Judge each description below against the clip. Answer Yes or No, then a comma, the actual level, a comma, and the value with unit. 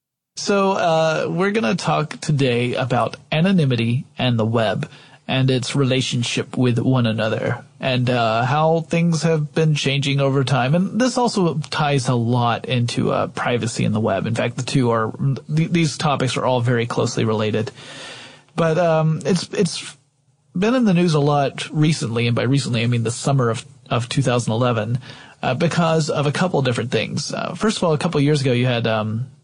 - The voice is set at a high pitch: No, medium, 140 Hz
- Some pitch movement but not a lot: Yes, average, 4.6 semitones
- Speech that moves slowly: No, average, 185 wpm